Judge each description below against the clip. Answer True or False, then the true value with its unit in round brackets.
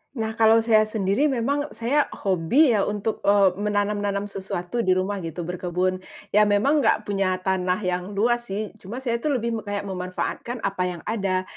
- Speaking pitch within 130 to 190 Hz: False (205 Hz)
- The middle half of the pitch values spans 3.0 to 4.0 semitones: True (3.6 semitones)